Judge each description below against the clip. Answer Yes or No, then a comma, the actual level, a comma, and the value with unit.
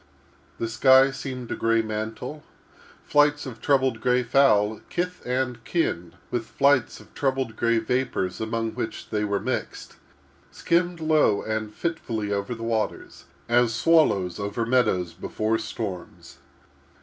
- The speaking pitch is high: No, low, 115 Hz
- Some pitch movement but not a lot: Yes, average, 3.6 semitones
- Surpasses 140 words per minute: No, slow, 135 wpm